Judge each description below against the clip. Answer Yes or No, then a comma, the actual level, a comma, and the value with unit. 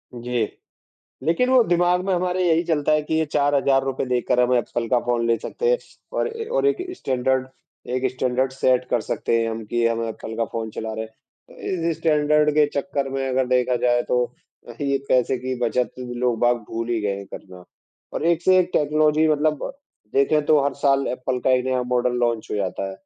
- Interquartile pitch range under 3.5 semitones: No, average, 4.0 semitones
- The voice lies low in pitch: Yes, low, 130 Hz